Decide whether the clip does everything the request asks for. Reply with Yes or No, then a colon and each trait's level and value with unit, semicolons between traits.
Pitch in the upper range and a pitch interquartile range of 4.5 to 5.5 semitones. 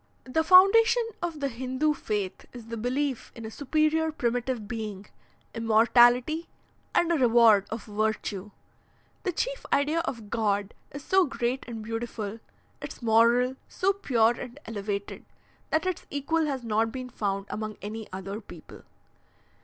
Yes: high, 240 Hz; average, 5.2 semitones